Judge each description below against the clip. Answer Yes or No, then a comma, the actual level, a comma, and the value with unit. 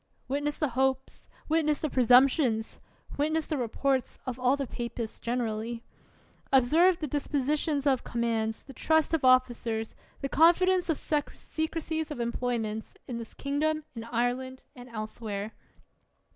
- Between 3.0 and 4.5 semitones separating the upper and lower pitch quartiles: Yes, average, 4.2 semitones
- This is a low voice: No, very high, 260 Hz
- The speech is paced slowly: Yes, slow, 130 wpm